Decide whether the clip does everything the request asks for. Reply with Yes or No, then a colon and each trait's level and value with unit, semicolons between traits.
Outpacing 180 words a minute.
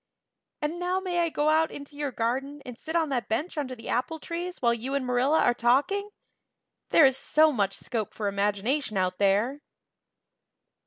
Yes: average, 190 wpm